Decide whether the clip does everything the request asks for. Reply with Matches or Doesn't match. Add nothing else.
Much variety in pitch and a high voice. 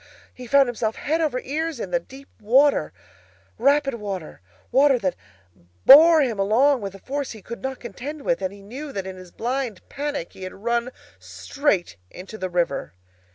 Matches